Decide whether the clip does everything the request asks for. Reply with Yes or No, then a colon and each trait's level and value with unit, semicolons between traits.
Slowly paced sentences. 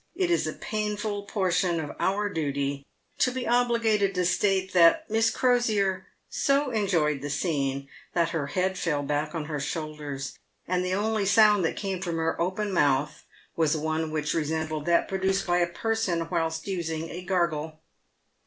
No: average, 165 wpm